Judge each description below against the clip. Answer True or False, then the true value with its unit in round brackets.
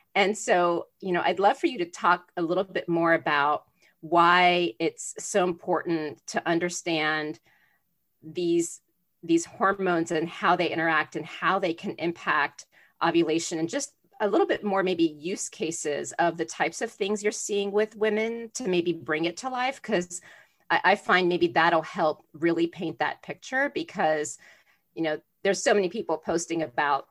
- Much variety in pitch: False (3.3 semitones)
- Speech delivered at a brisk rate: False (175 wpm)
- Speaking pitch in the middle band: True (175 Hz)